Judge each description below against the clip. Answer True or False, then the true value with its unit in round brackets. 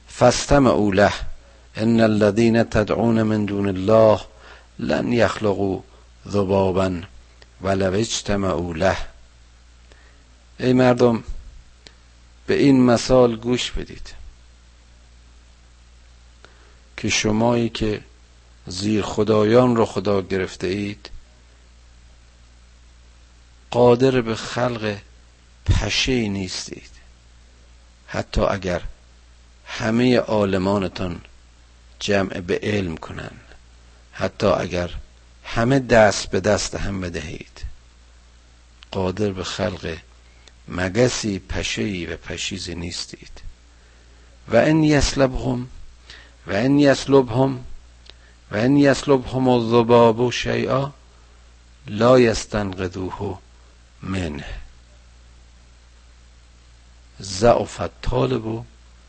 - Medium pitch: False (85 Hz)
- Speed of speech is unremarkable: False (80 wpm)